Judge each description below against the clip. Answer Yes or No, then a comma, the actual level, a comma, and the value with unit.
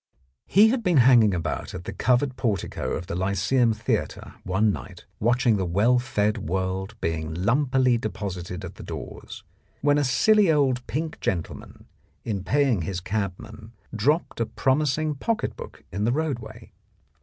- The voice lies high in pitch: No, low, 115 Hz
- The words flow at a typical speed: Yes, average, 155 wpm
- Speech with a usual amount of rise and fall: No, wide, 5.8 semitones